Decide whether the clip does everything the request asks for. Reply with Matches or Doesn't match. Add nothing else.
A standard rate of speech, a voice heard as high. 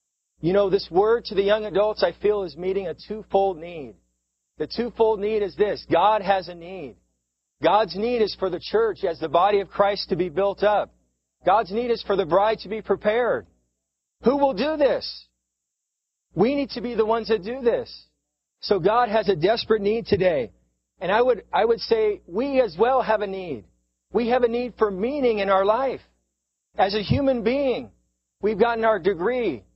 Matches